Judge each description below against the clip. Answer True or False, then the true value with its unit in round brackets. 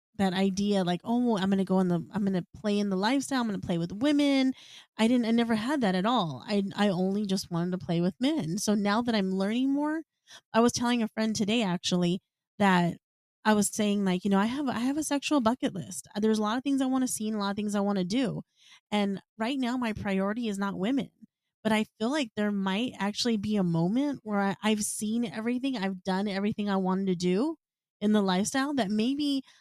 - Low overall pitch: False (210 Hz)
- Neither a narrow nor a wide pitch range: True (3.8 semitones)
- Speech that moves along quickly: True (245 wpm)